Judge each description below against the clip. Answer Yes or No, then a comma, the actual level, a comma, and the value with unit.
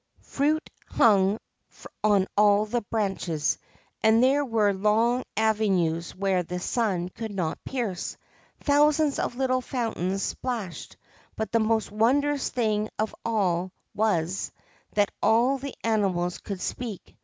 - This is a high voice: Yes, high, 215 Hz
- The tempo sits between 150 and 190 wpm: No, slow, 135 wpm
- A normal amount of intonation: Yes, average, 4.0 semitones